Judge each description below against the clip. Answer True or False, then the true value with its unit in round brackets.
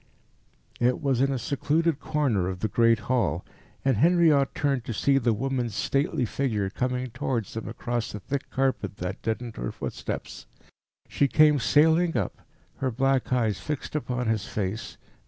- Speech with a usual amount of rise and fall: True (3.9 semitones)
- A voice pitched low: True (125 Hz)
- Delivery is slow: False (160 wpm)